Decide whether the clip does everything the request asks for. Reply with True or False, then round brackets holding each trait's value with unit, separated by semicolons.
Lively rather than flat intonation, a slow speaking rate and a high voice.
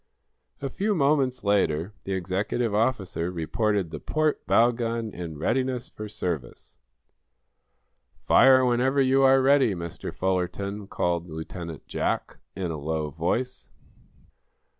False (6.8 semitones; 120 wpm; 105 Hz)